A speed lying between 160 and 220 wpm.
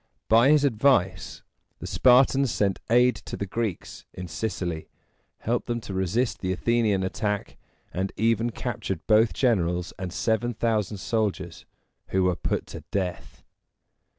No: average, 140 wpm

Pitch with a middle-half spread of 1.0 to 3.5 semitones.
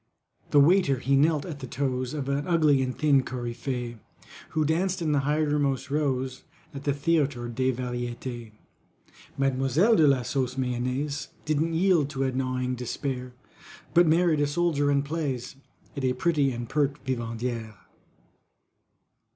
Yes: average, 3.0 semitones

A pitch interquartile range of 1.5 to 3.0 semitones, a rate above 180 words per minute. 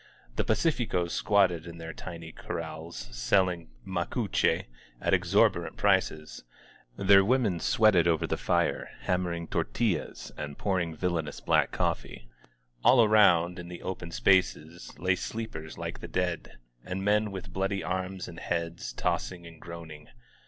No: average, 2.7 semitones; average, 140 wpm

